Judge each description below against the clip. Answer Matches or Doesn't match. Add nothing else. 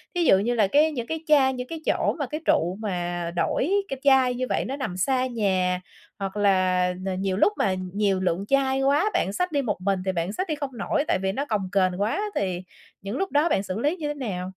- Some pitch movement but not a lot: Doesn't match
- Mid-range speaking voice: Doesn't match